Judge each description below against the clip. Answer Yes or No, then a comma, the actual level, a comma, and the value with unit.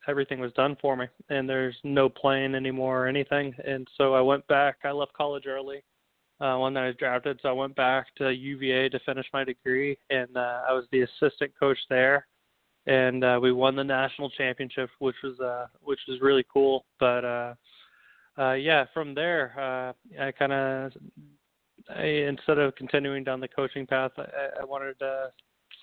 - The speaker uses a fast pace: No, average, 190 wpm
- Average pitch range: No, narrow, 1.2 semitones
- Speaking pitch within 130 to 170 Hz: Yes, low, 135 Hz